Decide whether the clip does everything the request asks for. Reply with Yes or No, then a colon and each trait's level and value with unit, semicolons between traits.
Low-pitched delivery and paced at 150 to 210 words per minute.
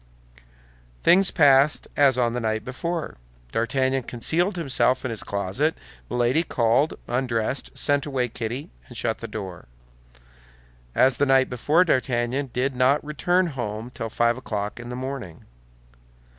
No: low, 130 Hz; average, 140 wpm